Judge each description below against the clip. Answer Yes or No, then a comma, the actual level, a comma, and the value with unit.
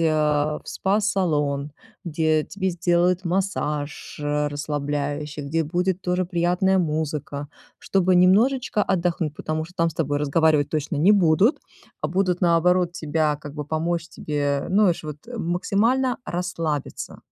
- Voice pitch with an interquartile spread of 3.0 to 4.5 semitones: Yes, average, 3.5 semitones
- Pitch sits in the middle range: Yes, medium, 165 Hz